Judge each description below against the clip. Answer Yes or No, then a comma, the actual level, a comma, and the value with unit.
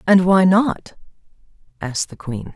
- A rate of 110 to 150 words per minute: Yes, average, 140 wpm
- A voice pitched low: No, medium, 180 Hz